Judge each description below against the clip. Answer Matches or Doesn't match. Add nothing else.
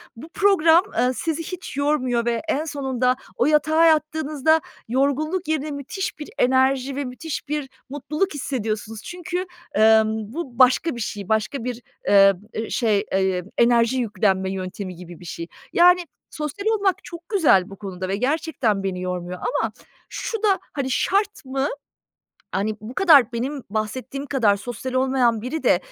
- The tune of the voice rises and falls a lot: Matches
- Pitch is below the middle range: Doesn't match